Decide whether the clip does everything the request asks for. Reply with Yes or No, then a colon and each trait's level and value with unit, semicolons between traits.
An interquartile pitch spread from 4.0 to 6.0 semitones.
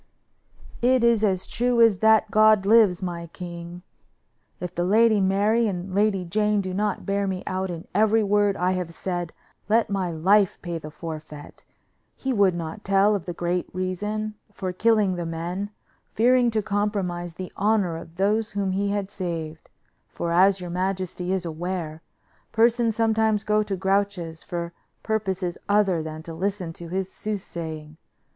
No: average, 3.2 semitones